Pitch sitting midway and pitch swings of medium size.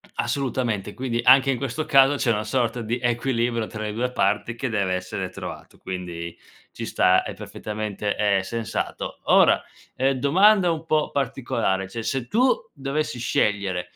No: low, 120 Hz; average, 4.4 semitones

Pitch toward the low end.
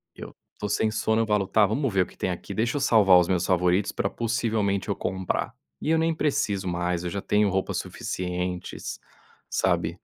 Yes: low, 100 Hz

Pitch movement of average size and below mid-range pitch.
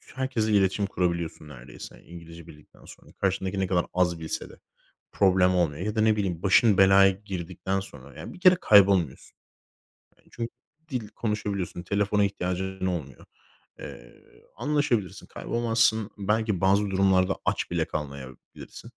Yes: average, 3.3 semitones; very low, 95 Hz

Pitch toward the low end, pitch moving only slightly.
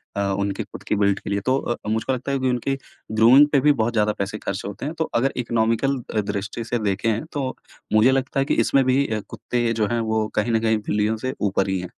No: low, 115 Hz; average, 3.7 semitones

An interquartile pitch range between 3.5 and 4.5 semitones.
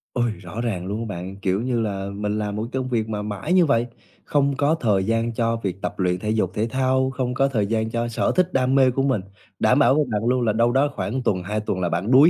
Yes: average, 3.9 semitones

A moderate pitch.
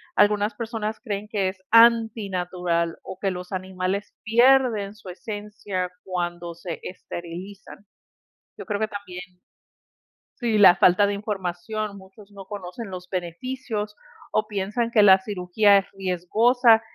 No: high, 200 Hz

